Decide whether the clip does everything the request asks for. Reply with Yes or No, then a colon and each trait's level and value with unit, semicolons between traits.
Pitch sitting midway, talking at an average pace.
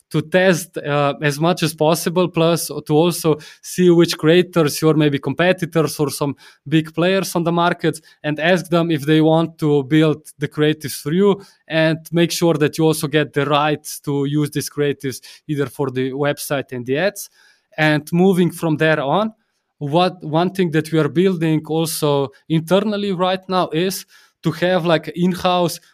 Yes: medium, 160 Hz; average, 180 wpm